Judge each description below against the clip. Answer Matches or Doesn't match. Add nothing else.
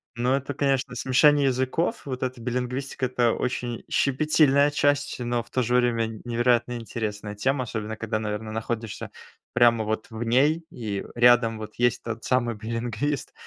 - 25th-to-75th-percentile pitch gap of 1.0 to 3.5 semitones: Matches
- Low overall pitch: Matches